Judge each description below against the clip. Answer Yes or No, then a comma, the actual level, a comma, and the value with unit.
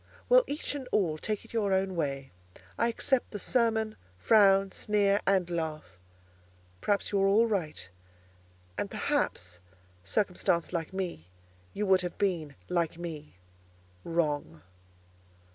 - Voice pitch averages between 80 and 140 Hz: No, high, 190 Hz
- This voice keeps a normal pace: No, slow, 130 wpm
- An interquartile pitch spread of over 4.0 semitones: Yes, average, 4.6 semitones